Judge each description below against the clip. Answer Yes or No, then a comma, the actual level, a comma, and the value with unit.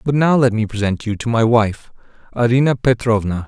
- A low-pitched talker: Yes, low, 115 Hz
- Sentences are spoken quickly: No, average, 190 wpm